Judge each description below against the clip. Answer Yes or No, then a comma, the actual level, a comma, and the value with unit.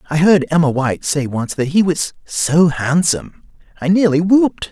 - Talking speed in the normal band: Yes, average, 180 wpm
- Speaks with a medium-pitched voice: Yes, medium, 160 Hz